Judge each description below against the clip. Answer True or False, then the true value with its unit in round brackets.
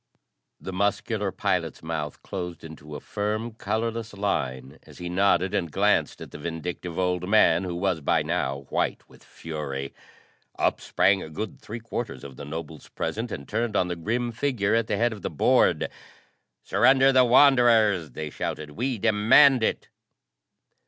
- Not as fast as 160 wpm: False (165 wpm)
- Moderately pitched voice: False (100 Hz)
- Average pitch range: False (5.8 semitones)